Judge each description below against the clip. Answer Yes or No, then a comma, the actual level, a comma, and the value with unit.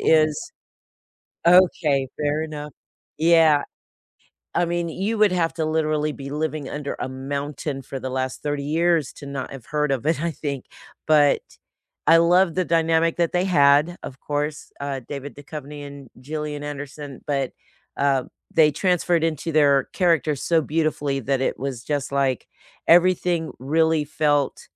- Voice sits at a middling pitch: Yes, medium, 150 Hz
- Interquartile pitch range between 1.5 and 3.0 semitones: Yes, average, 2.7 semitones